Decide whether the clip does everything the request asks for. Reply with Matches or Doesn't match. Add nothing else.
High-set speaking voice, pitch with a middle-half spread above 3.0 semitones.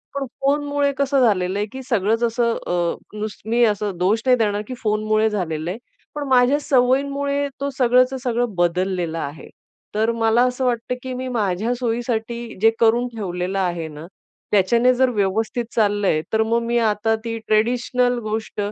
Matches